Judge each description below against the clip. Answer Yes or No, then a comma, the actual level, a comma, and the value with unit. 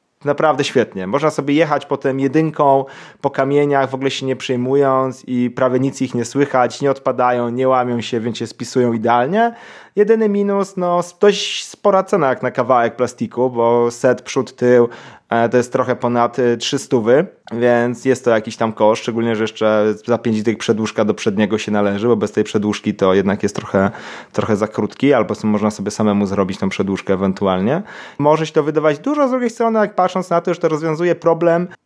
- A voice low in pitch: Yes, low, 125 Hz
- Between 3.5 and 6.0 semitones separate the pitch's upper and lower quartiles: Yes, average, 4.8 semitones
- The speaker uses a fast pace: Yes, fast, 190 wpm